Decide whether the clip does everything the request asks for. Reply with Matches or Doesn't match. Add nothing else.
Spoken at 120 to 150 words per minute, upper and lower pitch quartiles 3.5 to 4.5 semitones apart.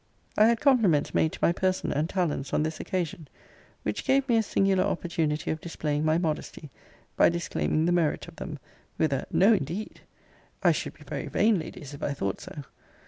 Doesn't match